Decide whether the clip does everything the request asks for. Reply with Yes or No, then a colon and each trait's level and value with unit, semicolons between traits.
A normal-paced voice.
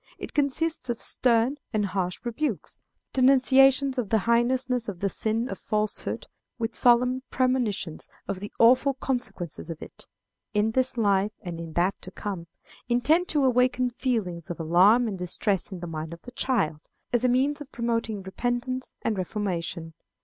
Yes: average, 165 wpm